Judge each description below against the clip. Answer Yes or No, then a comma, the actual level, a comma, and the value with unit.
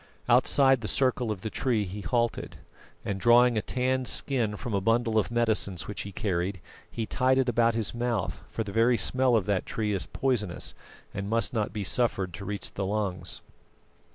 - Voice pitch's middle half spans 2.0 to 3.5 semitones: Yes, average, 3.2 semitones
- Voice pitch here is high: No, low, 110 Hz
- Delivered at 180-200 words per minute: Yes, average, 190 wpm